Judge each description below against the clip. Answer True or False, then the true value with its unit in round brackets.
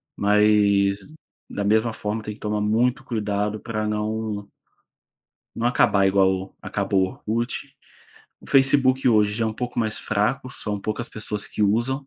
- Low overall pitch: True (105 Hz)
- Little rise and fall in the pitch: True (2.2 semitones)